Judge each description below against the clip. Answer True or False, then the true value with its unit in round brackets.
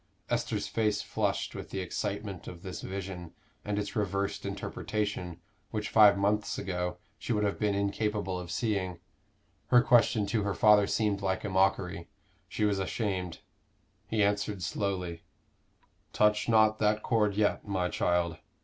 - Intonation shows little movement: True (2.2 semitones)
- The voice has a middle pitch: False (100 Hz)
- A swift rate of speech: False (150 wpm)